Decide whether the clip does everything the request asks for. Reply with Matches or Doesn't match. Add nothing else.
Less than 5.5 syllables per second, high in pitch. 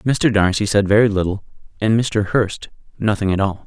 Doesn't match